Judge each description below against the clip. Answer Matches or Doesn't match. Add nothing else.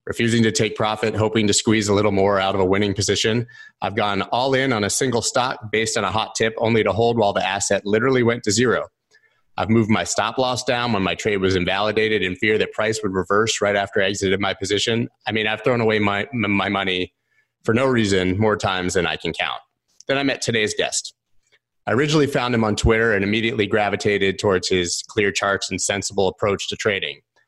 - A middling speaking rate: Doesn't match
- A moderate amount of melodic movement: Doesn't match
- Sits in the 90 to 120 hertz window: Matches